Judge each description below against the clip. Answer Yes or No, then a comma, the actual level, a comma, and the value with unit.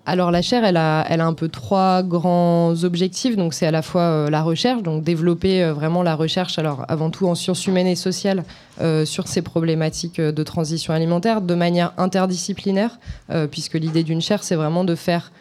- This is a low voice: No, medium, 175 Hz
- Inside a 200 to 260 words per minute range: Yes, average, 210 wpm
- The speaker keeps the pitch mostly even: Yes, narrow, 2.3 semitones